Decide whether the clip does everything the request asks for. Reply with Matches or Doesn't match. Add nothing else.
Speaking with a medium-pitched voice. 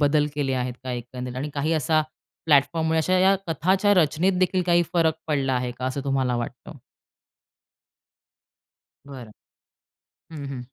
Matches